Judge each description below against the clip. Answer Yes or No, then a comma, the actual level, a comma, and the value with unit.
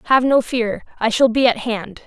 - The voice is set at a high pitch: Yes, high, 230 Hz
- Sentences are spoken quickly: Yes, fast, 235 wpm